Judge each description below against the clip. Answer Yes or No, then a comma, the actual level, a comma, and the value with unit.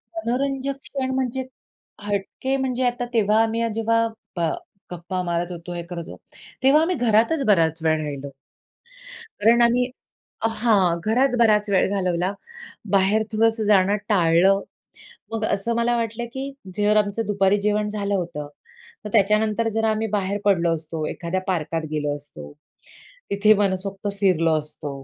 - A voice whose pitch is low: No, high, 205 Hz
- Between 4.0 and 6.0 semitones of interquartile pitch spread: Yes, average, 4.5 semitones